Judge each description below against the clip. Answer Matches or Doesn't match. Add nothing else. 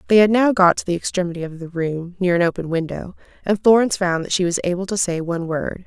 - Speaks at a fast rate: Matches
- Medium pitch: Matches